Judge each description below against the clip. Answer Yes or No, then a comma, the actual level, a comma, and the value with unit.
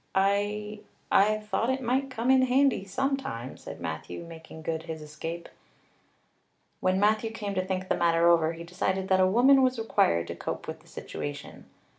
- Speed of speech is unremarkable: Yes, average, 175 wpm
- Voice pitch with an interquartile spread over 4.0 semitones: Yes, average, 5.3 semitones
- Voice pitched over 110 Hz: Yes, high, 190 Hz